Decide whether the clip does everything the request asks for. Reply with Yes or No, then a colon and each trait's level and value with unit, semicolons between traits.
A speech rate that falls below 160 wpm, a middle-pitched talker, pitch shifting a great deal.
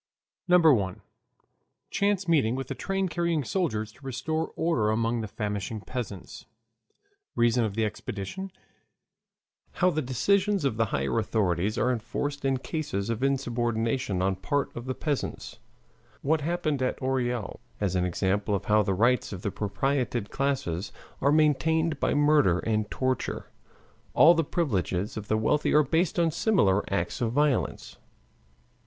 No: average, 150 wpm; low, 125 Hz; wide, 6.2 semitones